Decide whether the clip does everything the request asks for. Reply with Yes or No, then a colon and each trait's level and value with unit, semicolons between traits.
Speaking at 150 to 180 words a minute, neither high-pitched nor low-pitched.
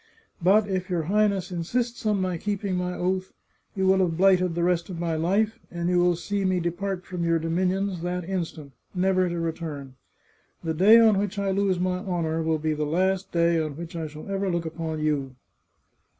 No: fast, 205 wpm; medium, 180 Hz